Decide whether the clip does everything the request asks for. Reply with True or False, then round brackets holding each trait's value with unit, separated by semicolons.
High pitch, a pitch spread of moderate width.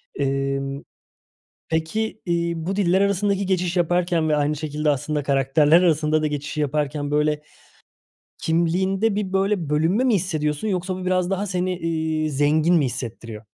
False (160 Hz; 3.8 semitones)